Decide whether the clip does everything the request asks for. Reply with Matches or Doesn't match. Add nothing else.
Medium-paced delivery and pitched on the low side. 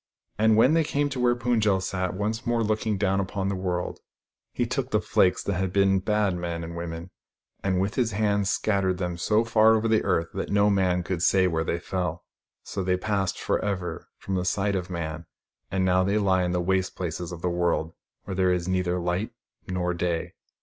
Doesn't match